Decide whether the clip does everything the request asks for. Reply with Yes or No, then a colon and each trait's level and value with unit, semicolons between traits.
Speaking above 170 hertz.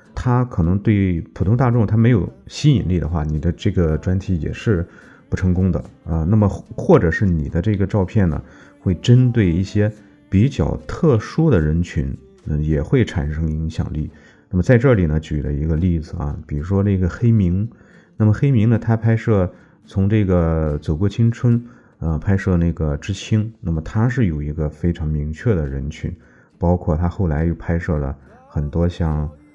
No: very low, 90 Hz